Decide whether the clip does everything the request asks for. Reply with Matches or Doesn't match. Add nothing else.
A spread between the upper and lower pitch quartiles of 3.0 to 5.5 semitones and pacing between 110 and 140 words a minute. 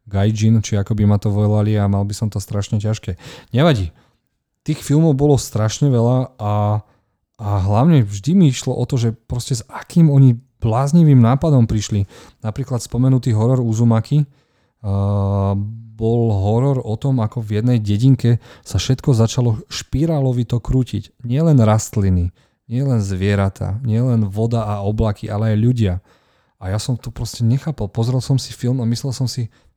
Doesn't match